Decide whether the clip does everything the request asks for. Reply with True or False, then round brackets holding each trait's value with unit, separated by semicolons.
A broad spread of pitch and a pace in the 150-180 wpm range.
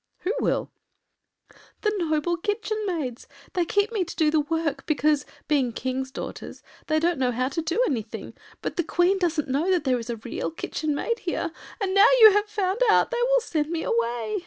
False (6.0 semitones; 205 wpm)